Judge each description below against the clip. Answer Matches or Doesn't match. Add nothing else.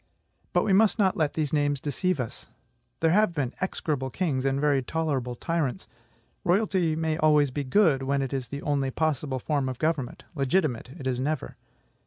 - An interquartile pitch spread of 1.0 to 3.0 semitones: Doesn't match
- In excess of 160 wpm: Matches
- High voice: Doesn't match